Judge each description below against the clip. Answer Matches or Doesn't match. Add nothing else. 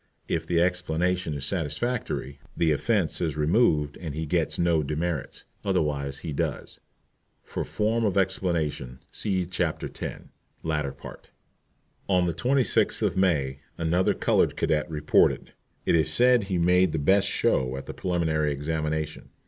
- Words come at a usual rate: Matches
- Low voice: Matches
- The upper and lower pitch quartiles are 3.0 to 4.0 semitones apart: Matches